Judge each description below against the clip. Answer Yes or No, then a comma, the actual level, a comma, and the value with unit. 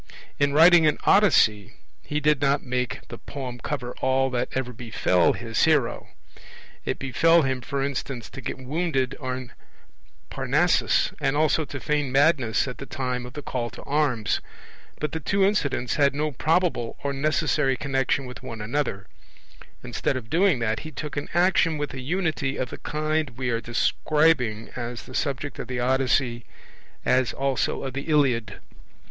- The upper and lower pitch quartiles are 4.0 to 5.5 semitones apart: No, average, 3.3 semitones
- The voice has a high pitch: No, low, 135 Hz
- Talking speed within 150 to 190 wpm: Yes, average, 165 wpm